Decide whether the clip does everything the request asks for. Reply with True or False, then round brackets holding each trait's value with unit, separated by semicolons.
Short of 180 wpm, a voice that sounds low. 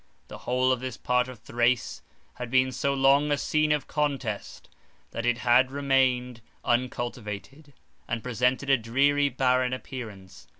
True (145 wpm; 125 Hz)